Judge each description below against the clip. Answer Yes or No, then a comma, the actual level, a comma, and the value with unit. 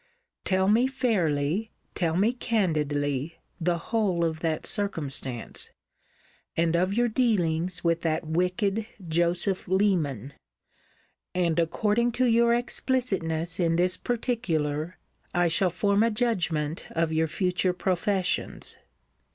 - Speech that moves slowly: Yes, slow, 115 wpm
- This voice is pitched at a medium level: Yes, medium, 180 Hz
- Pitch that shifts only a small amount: No, average, 4.5 semitones